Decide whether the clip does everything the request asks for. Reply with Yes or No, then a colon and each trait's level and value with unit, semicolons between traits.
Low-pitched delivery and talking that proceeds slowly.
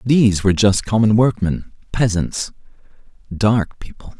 Yes: low, 105 Hz; slow, 115 wpm